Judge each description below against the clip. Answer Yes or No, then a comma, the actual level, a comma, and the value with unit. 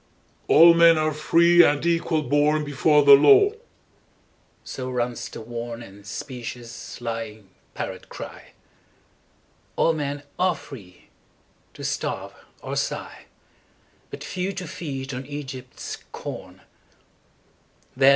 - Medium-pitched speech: Yes, medium, 145 Hz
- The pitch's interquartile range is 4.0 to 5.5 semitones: Yes, average, 5.1 semitones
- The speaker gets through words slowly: Yes, slow, 95 wpm